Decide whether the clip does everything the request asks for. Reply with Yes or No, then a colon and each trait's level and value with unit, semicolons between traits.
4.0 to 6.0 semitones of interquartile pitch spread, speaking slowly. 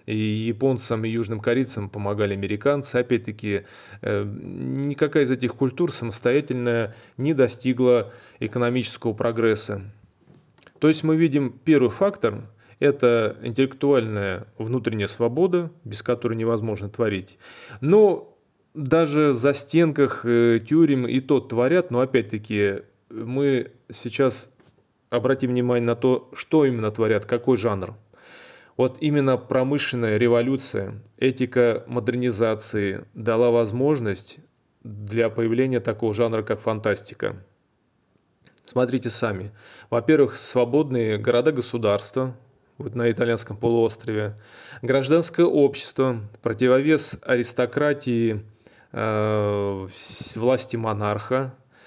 No: average, 3.4 semitones; slow, 95 wpm